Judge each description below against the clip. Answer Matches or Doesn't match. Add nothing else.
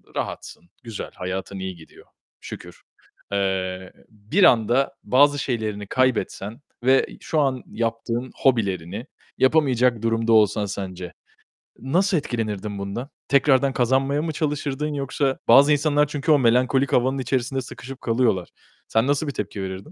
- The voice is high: Doesn't match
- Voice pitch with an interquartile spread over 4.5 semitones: Matches